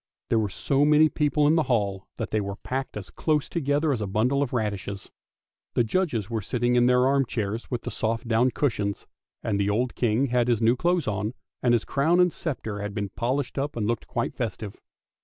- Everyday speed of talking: No, fast, 215 wpm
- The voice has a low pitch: Yes, low, 120 Hz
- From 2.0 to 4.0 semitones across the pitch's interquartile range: No, average, 4.7 semitones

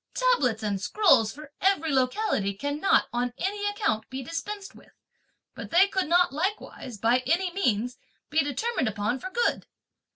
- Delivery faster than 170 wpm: No, average, 155 wpm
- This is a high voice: Yes, very high, 300 Hz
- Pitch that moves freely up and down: Yes, wide, 8.0 semitones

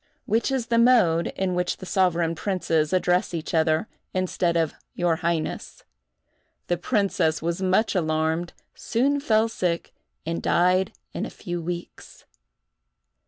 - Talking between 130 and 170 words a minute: Yes, slow, 135 wpm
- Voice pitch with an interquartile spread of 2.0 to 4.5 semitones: Yes, average, 2.8 semitones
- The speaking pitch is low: No, medium, 175 Hz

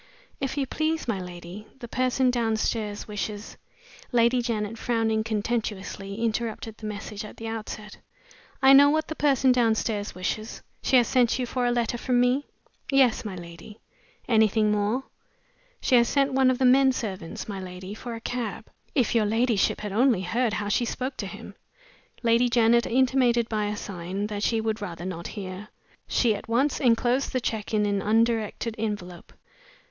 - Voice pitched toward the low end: No, high, 225 Hz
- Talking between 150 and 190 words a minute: Yes, average, 175 wpm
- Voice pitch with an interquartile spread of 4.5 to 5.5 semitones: No, average, 3.1 semitones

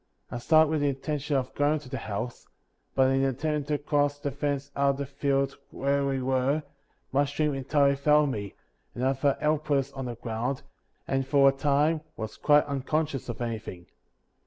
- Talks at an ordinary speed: Yes, average, 185 wpm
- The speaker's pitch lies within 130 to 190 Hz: Yes, medium, 140 Hz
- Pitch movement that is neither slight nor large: No, narrow, 1.8 semitones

